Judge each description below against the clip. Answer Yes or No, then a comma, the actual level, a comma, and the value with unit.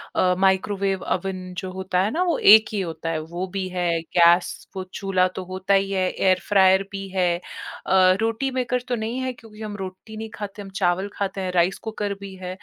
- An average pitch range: No, narrow, 2.3 semitones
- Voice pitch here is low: No, high, 190 Hz